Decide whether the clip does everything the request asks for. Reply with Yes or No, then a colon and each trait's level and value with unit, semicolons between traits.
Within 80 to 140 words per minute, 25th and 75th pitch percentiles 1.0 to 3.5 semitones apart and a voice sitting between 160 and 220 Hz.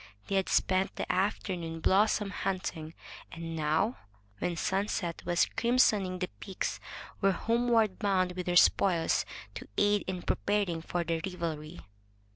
Yes: slow, 135 wpm; average, 3.1 semitones; medium, 185 Hz